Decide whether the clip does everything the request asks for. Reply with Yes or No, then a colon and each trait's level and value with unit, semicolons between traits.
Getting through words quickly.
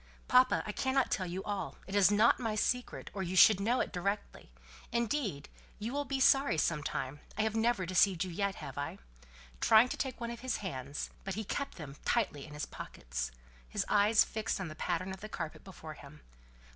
Yes: fast, 210 wpm